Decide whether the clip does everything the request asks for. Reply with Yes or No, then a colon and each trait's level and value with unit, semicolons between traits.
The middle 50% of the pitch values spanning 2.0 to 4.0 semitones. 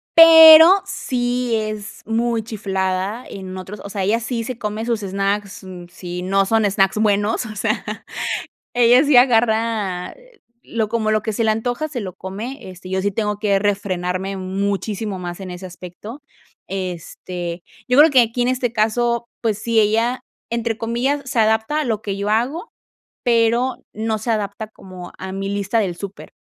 Yes: average, 3.4 semitones